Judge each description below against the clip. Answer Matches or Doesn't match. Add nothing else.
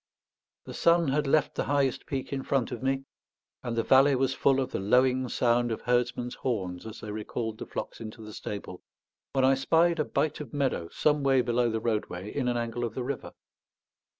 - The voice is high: Doesn't match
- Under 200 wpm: Doesn't match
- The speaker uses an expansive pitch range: Doesn't match